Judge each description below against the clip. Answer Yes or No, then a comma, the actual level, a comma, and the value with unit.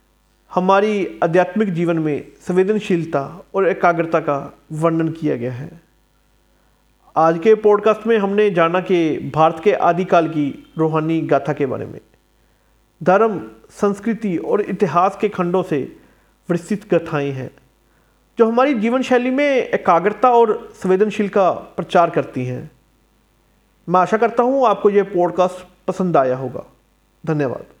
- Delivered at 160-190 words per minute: No, average, 130 wpm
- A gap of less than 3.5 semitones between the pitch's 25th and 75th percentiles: No, average, 4.8 semitones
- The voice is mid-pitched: Yes, medium, 180 Hz